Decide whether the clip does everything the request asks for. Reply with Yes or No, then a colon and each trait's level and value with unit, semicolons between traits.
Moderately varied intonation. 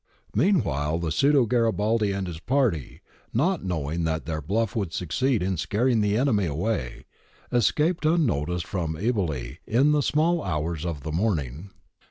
No: wide, 7.5 semitones